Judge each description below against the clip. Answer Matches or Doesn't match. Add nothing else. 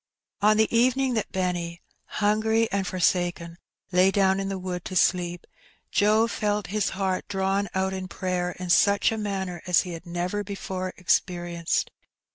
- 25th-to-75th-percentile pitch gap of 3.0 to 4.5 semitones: Doesn't match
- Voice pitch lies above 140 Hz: Matches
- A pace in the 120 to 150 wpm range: Doesn't match